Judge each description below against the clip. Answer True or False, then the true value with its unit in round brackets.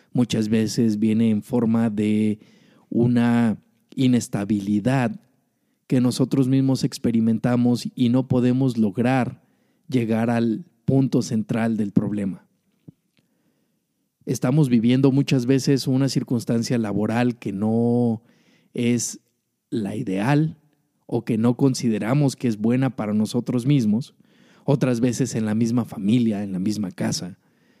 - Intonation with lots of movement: False (2.9 semitones)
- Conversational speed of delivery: False (115 wpm)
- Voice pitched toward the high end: False (120 Hz)